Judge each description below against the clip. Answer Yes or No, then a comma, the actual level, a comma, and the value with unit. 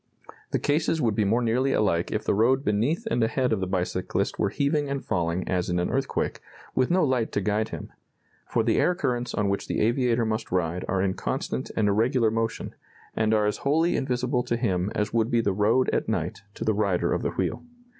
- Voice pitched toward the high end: No, low, 110 Hz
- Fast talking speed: Yes, fast, 220 wpm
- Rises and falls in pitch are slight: No, average, 4.0 semitones